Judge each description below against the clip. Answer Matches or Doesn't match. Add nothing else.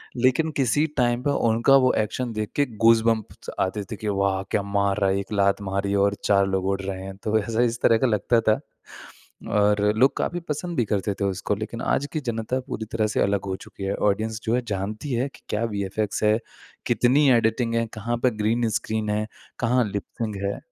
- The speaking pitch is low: Matches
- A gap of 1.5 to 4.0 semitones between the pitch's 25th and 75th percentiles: Matches